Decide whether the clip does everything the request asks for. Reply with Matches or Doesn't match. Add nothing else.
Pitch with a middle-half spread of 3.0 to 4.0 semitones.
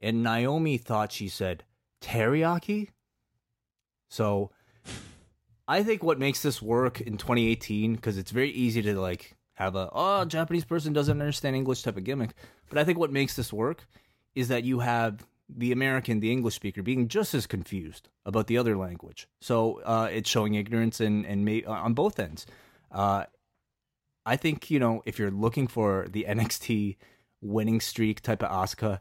Matches